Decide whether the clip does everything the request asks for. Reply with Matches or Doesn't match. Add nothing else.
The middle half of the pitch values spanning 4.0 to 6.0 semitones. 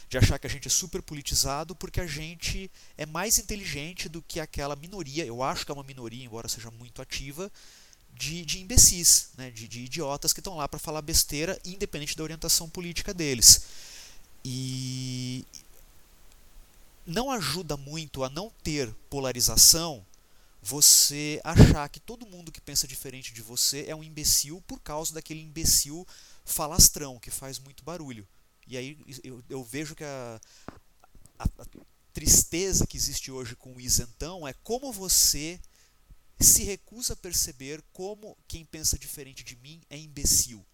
Matches